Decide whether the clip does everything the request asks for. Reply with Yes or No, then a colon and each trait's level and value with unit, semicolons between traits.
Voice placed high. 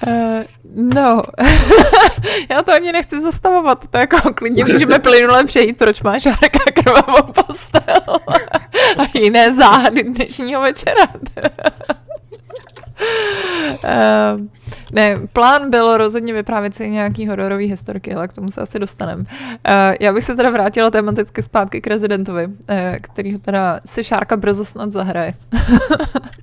Yes: high, 235 Hz